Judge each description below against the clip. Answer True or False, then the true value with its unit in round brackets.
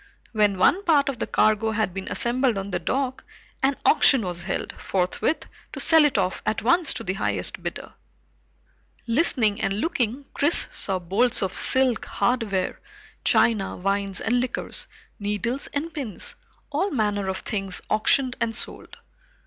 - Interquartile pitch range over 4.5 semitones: True (5.2 semitones)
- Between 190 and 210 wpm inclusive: False (155 wpm)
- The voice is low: False (220 Hz)